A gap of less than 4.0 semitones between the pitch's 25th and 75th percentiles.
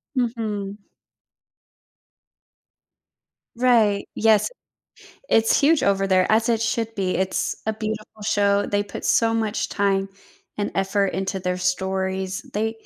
Yes: narrow, 2.5 semitones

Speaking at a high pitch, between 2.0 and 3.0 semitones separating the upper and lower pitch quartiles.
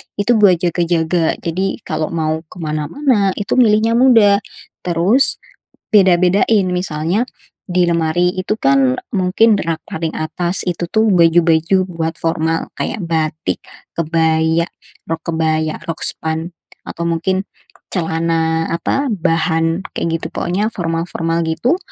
No: medium, 170 Hz; average, 2.7 semitones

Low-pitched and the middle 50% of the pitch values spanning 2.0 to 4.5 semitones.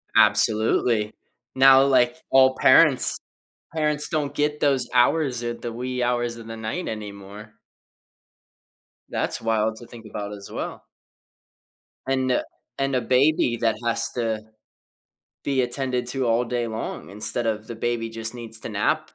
Yes: low, 120 Hz; average, 2.7 semitones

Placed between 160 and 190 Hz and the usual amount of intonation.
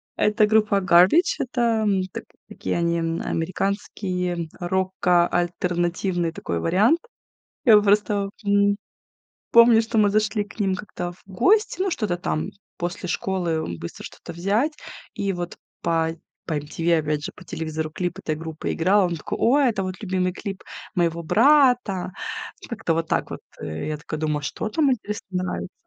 Yes: medium, 185 Hz; average, 3.8 semitones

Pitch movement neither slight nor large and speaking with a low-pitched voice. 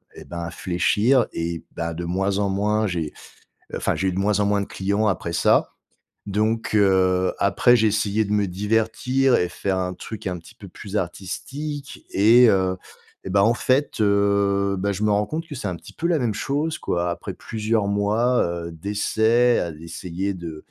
Yes: average, 3.2 semitones; low, 100 Hz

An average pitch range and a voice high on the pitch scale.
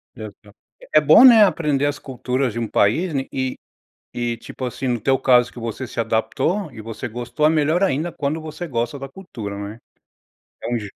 No: average, 4.6 semitones; low, 130 Hz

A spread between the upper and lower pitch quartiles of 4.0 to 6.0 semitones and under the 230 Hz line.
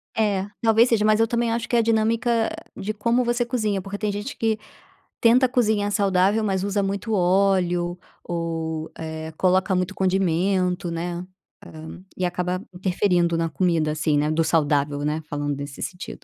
Yes: average, 4.3 semitones; high, 190 Hz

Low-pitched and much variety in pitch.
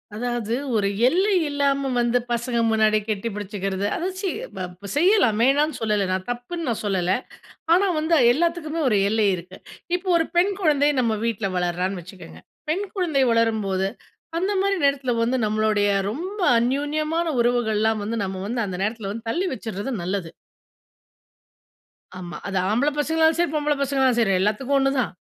No: high, 235 Hz; wide, 6.4 semitones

